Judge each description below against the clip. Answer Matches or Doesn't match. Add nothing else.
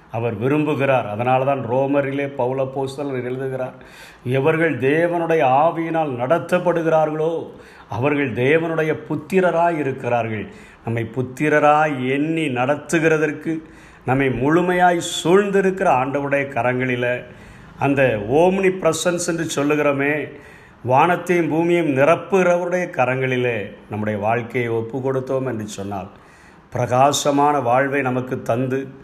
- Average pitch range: Matches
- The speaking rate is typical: Matches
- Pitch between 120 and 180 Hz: Matches